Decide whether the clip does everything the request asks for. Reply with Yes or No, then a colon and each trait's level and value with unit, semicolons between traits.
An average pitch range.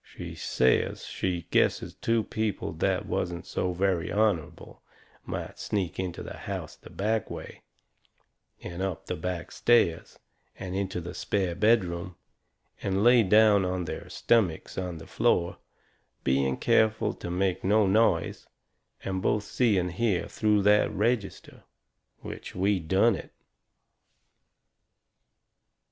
Yes: average, 3.3 semitones